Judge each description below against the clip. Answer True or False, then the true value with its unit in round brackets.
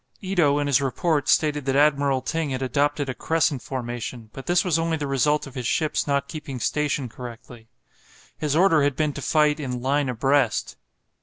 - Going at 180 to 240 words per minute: True (185 wpm)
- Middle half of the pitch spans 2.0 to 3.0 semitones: True (2.6 semitones)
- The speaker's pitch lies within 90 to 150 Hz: True (140 Hz)